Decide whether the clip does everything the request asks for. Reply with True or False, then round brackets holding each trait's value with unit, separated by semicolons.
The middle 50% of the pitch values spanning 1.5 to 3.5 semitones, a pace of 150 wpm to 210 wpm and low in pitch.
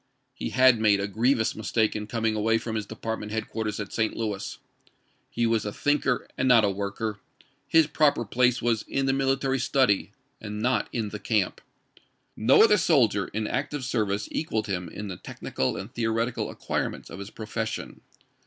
True (3.0 semitones; 180 wpm; 110 Hz)